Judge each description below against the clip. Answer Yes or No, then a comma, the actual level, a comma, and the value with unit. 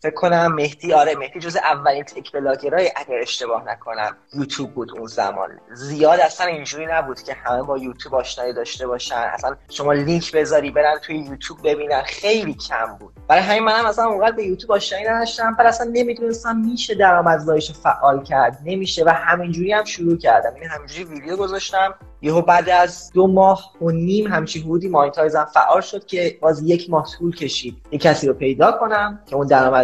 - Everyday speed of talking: No, fast, 180 wpm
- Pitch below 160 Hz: No, medium, 165 Hz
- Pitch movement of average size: Yes, average, 5.0 semitones